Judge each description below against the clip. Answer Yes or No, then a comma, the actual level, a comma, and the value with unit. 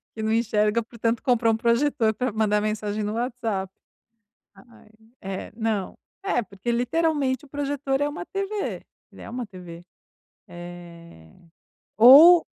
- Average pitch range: Yes, average, 4.1 semitones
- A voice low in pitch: No, high, 230 Hz